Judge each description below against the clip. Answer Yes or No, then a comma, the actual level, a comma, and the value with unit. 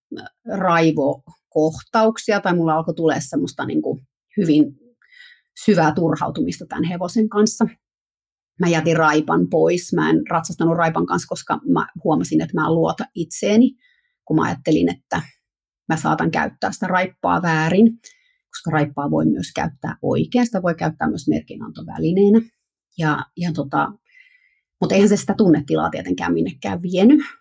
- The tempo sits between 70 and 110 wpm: No, average, 135 wpm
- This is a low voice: No, medium, 180 Hz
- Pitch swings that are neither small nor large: No, wide, 6.3 semitones